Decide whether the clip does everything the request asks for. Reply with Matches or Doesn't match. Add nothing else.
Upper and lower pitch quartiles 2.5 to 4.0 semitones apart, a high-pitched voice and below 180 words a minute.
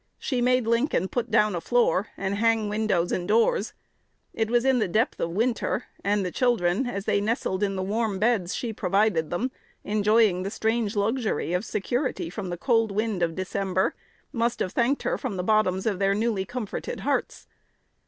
Doesn't match